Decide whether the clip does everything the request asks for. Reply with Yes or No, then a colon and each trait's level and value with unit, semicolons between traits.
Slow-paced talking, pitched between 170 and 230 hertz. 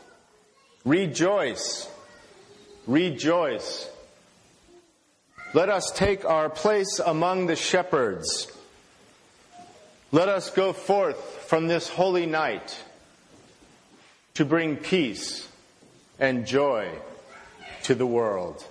Yes: slow, 85 wpm; medium, 185 Hz